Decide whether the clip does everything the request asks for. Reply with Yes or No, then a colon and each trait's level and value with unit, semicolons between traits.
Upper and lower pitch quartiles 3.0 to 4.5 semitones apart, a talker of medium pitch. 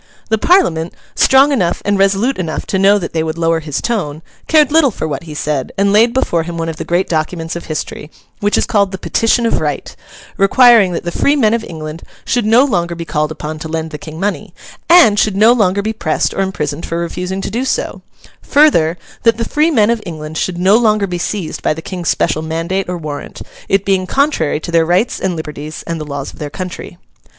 No: average, 5.2 semitones; medium, 180 Hz